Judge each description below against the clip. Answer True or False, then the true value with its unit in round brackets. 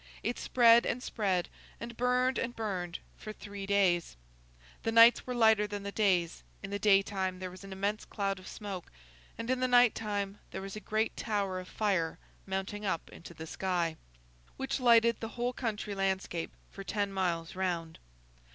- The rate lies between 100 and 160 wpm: False (180 wpm)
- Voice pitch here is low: False (200 Hz)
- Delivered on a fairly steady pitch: False (3.2 semitones)